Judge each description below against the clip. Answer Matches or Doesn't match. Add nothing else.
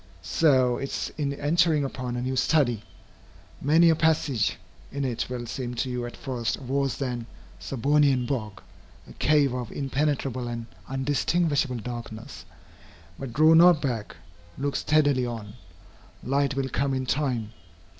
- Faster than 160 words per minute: Doesn't match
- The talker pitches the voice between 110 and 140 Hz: Matches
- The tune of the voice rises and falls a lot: Doesn't match